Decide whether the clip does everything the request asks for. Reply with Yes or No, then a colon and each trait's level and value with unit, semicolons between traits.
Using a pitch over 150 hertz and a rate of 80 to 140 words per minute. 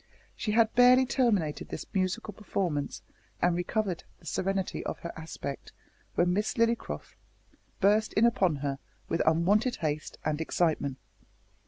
Yes: medium, 185 Hz; slow, 135 wpm